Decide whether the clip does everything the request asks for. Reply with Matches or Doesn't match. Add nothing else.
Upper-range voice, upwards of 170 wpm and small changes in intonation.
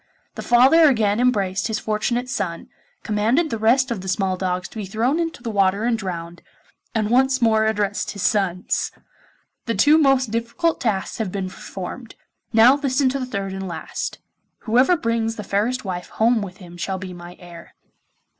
Doesn't match